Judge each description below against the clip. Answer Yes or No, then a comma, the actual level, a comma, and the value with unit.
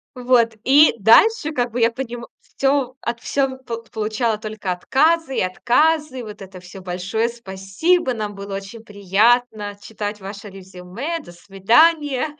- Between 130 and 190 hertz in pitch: No, high, 230 Hz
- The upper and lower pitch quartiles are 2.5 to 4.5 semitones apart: No, average, 4.9 semitones